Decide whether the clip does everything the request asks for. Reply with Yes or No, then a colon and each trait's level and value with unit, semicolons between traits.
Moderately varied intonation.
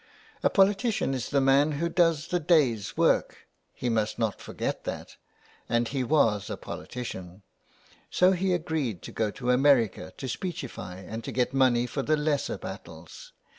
No: wide, 5.7 semitones